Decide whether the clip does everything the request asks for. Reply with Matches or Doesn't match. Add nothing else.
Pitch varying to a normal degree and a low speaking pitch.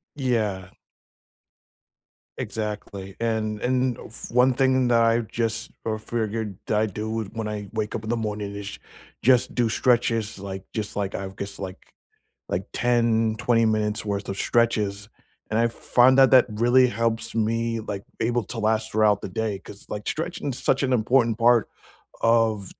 Doesn't match